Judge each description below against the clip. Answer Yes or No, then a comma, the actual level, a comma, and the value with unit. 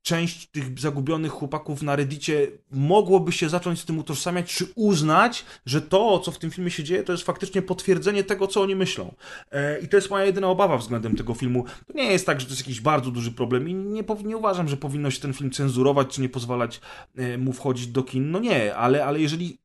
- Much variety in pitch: Yes, wide, 5.7 semitones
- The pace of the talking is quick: Yes, fast, 220 wpm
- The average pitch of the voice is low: No, medium, 155 Hz